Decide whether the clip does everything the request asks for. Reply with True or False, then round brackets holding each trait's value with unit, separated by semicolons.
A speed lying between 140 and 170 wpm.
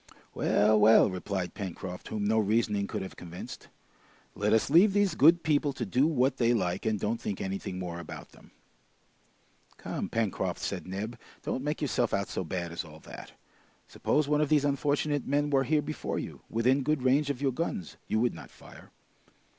False (185 wpm)